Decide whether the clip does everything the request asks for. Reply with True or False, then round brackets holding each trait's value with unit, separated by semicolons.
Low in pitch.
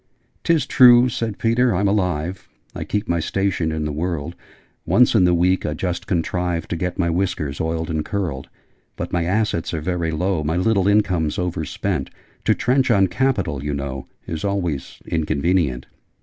True (90 Hz)